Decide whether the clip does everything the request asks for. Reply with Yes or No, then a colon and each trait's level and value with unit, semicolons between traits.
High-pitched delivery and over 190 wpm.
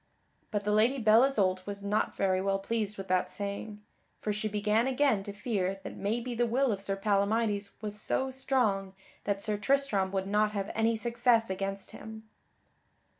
No: high, 210 Hz; average, 175 wpm